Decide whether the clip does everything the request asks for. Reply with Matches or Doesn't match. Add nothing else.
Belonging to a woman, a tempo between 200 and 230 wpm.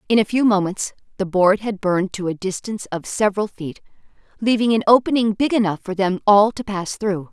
Matches